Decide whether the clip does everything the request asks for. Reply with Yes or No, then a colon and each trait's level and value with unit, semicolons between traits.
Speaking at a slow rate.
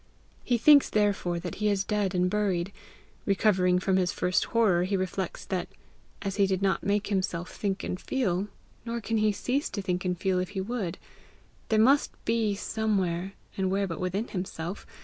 No: average, 180 wpm